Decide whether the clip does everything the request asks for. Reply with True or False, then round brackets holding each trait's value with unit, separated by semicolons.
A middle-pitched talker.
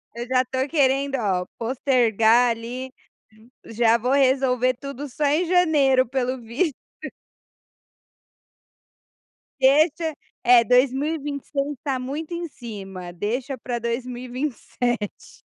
False (255 Hz)